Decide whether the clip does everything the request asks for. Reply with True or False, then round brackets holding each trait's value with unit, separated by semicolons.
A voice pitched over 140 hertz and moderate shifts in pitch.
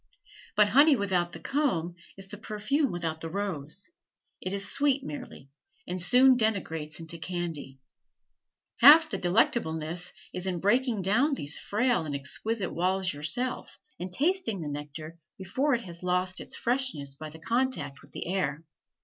False (190 Hz; 7.0 semitones)